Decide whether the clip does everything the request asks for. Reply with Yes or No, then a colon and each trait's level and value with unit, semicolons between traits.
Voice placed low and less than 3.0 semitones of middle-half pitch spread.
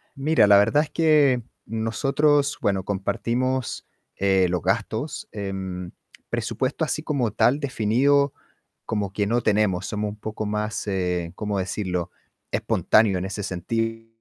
No: low, 105 Hz; average, 4.7 semitones